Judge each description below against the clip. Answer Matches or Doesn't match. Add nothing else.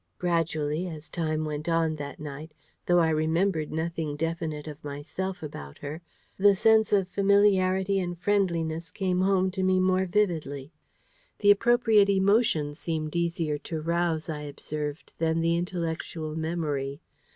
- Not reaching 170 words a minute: Matches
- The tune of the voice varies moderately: Matches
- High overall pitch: Doesn't match